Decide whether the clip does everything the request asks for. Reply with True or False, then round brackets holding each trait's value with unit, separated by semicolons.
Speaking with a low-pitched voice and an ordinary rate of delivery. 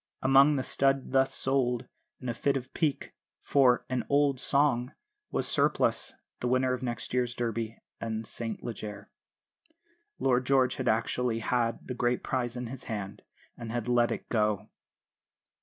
True (125 Hz; 160 wpm)